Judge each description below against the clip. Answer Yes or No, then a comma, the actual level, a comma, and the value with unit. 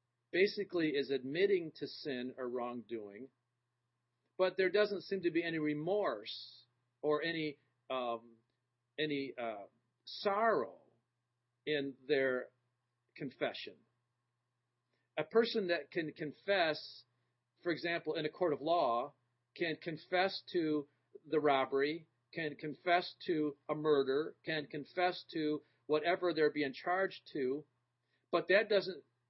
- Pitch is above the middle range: No, medium, 145 Hz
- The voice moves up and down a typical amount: No, wide, 5.9 semitones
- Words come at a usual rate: No, slow, 115 wpm